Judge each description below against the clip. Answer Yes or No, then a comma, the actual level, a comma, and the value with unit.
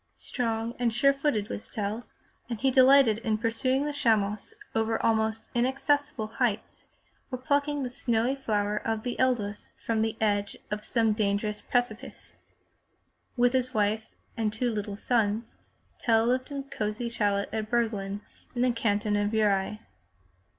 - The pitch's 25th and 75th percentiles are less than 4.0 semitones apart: Yes, average, 2.9 semitones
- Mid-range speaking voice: No, high, 225 Hz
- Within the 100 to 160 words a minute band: Yes, average, 150 wpm